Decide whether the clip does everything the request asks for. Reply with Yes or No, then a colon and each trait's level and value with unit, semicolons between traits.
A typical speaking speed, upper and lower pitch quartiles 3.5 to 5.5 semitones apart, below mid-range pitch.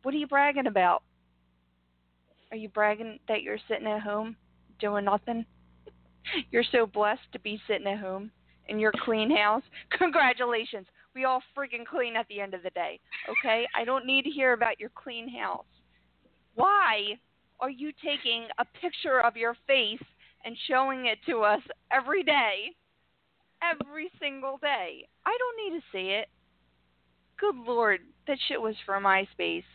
No: average, 160 wpm; average, 5.2 semitones; high, 225 Hz